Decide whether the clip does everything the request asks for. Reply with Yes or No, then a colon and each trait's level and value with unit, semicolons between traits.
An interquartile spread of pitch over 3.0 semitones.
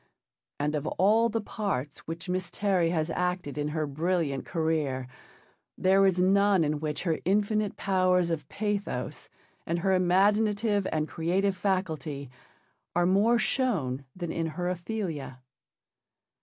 Yes: average, 4.1 semitones